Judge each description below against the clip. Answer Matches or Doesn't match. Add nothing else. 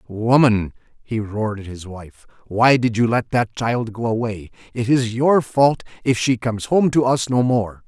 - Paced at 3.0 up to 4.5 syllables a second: Matches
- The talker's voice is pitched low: Matches